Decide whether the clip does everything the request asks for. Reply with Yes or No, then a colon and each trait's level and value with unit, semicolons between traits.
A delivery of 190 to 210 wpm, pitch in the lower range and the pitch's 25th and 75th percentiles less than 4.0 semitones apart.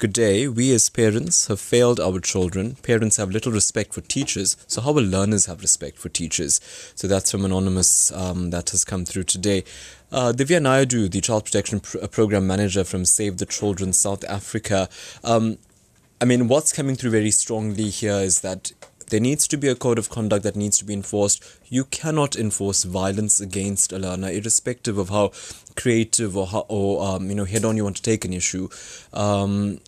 Yes: average, 195 wpm; low, 105 Hz; average, 2.9 semitones